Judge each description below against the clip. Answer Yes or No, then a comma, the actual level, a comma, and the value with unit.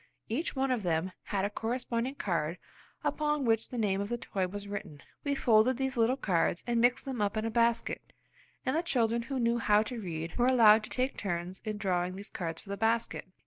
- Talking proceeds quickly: Yes, fast, 220 wpm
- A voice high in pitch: Yes, high, 225 Hz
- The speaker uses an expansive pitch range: No, average, 3.9 semitones